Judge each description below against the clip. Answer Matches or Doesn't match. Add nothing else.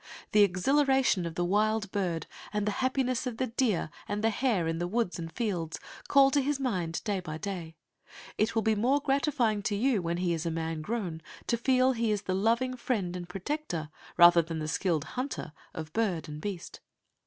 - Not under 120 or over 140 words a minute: Doesn't match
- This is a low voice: Doesn't match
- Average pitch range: Doesn't match